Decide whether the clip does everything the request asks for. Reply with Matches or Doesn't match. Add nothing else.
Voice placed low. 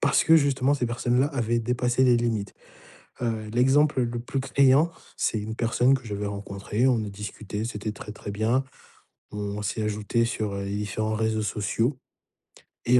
Matches